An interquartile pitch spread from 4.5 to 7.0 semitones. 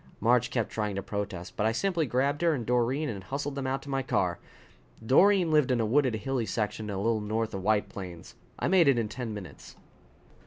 Yes: average, 4.8 semitones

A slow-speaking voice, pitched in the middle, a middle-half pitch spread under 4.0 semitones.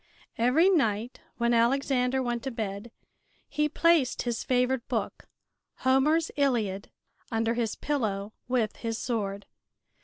No: slow, 120 wpm; high, 240 Hz; average, 3.1 semitones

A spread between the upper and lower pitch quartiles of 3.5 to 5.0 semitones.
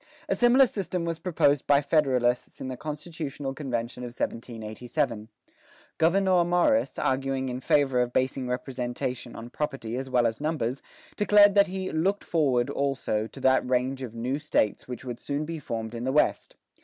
Yes: average, 4.5 semitones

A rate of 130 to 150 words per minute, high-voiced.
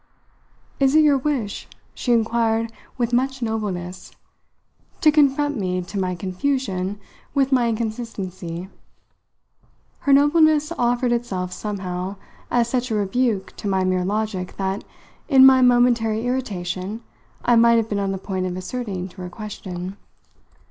Yes: average, 140 wpm; high, 220 Hz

